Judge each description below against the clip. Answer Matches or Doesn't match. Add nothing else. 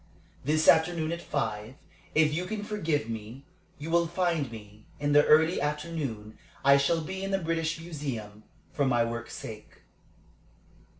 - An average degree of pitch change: Doesn't match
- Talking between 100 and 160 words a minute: Matches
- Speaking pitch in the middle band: Matches